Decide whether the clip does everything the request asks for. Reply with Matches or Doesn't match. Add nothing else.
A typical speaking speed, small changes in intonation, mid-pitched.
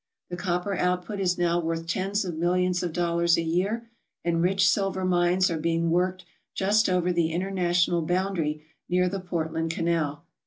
Matches